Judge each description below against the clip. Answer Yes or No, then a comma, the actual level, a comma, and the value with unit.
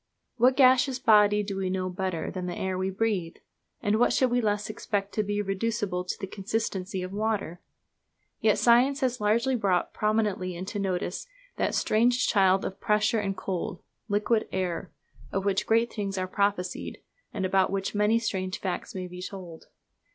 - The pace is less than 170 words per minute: No, average, 175 wpm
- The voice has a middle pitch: No, high, 200 Hz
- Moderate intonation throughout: Yes, average, 3.0 semitones